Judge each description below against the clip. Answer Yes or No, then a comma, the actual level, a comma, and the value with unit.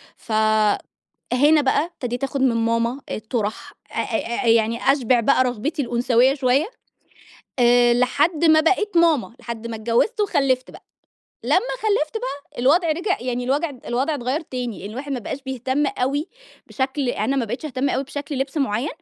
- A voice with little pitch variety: No, average, 3.6 semitones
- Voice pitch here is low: No, very high, 260 Hz